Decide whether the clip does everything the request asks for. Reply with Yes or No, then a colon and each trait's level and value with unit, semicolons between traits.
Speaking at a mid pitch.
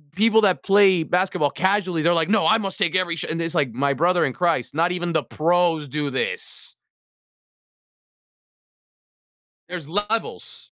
Yes: medium, 175 Hz